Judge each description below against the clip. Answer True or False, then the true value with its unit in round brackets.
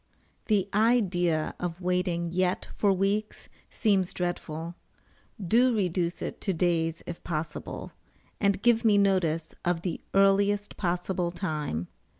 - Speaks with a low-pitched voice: False (180 Hz)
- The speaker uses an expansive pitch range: False (2.9 semitones)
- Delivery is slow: True (125 wpm)